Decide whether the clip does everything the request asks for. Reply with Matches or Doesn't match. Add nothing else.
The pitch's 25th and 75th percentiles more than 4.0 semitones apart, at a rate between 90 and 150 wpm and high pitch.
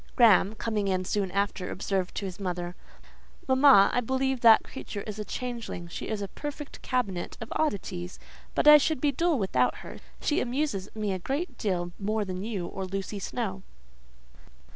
Doesn't match